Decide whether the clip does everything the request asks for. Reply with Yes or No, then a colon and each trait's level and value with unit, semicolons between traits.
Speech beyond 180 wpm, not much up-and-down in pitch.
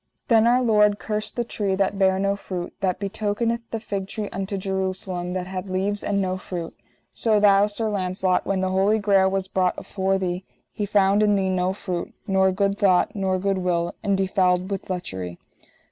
Yes: average, 190 wpm; narrow, 1.7 semitones